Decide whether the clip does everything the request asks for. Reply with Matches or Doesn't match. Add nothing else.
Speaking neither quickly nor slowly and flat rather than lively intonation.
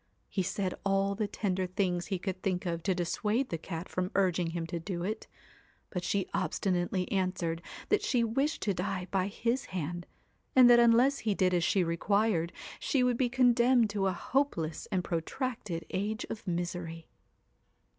Doesn't match